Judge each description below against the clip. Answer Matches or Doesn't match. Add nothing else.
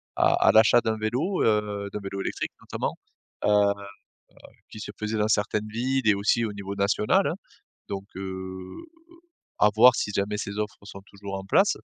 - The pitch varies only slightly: Matches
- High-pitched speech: Doesn't match